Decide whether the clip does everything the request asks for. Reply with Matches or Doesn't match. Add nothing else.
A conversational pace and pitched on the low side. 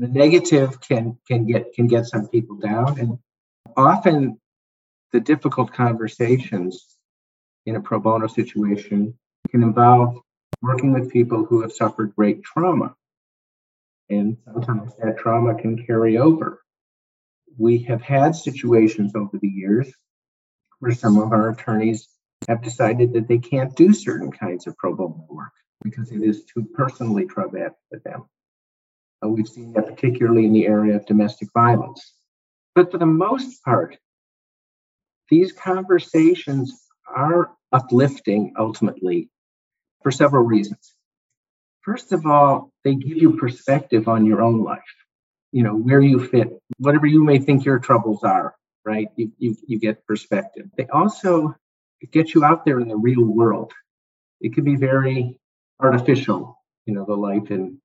Matches